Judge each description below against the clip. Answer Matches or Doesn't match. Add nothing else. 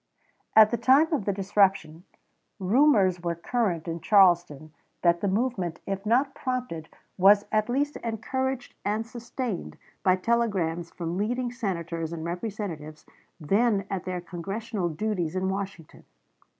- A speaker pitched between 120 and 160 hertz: Doesn't match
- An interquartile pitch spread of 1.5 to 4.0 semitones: Doesn't match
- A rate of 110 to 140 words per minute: Matches